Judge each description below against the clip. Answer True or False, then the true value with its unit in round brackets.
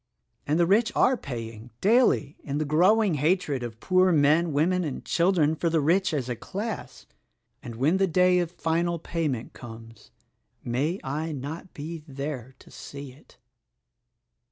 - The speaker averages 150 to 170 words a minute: True (160 wpm)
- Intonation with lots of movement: False (4.8 semitones)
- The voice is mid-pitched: True (155 Hz)